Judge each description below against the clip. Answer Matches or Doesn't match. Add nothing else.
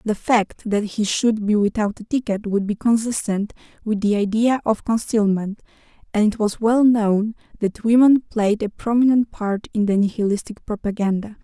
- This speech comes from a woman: Matches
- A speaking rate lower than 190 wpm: Matches